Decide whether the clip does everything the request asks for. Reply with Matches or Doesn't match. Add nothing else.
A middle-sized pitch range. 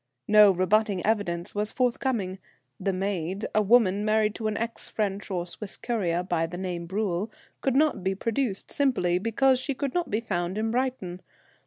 Matches